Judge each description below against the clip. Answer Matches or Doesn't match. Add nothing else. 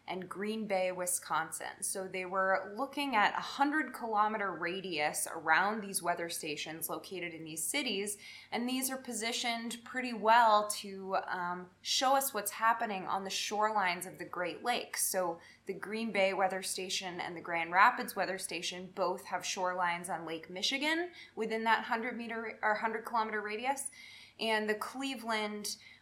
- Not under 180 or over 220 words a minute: Doesn't match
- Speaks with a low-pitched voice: Doesn't match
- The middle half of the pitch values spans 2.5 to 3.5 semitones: Doesn't match